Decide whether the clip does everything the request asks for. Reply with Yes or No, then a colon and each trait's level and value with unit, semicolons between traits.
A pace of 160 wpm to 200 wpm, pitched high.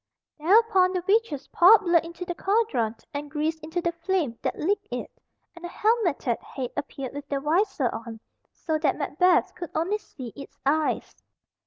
Yes: average, 170 wpm; very high, 330 Hz